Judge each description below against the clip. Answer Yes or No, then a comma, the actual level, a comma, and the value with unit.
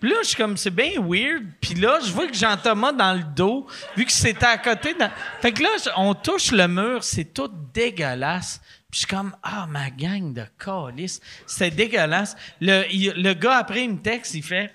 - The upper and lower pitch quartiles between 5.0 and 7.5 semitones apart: No, average, 4.6 semitones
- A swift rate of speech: Yes, fast, 225 wpm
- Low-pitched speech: No, high, 200 Hz